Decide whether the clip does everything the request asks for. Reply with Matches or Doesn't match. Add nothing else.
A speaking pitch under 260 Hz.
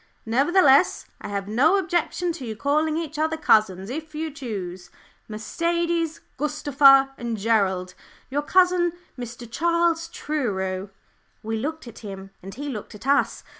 Doesn't match